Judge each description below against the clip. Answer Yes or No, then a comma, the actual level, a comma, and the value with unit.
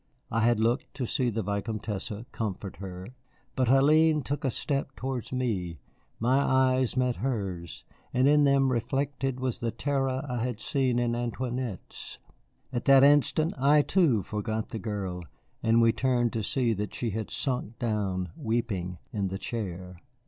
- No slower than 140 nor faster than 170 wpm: Yes, average, 160 wpm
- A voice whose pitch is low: Yes, low, 120 Hz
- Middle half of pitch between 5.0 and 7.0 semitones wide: No, average, 3.9 semitones